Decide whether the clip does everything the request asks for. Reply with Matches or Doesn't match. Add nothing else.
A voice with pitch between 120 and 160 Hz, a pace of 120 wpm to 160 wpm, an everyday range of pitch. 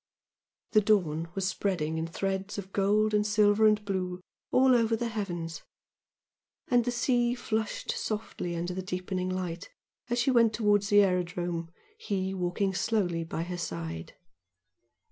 Doesn't match